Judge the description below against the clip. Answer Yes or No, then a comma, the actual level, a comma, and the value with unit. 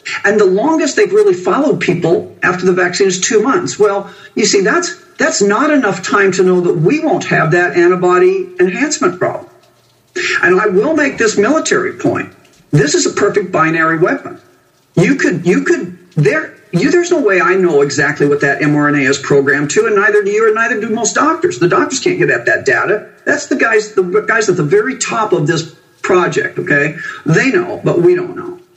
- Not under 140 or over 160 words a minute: No, average, 200 wpm